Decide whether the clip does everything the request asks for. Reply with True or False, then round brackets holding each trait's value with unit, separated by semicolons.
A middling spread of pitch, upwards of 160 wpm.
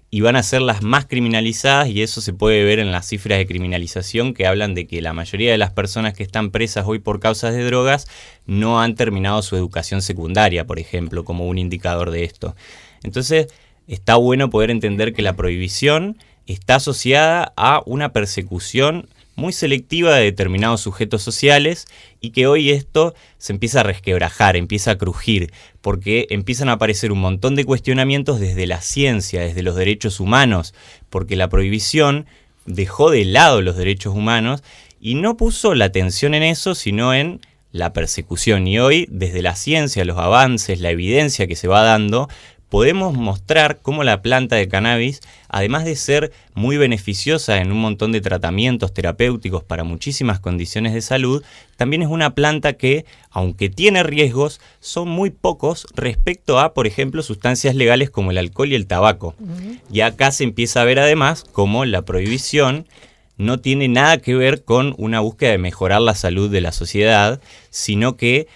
False (5.7 semitones; 175 wpm)